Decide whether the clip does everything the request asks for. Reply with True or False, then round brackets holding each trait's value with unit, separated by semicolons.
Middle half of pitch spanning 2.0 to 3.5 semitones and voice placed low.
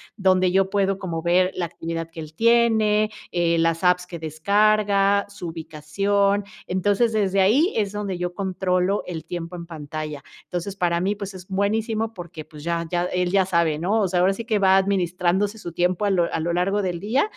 False (2.9 semitones; 185 Hz)